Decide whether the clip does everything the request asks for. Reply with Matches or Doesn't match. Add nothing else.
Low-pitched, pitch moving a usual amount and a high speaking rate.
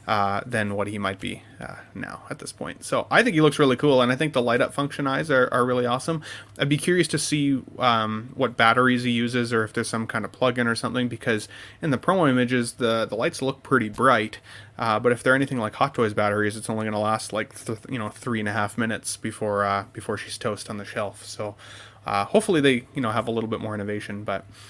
Matches